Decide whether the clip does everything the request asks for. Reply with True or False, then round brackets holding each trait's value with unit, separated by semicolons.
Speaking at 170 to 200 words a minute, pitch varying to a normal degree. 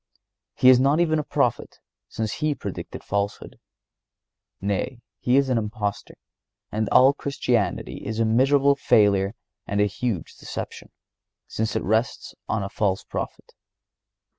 False (140 wpm; 4.5 semitones)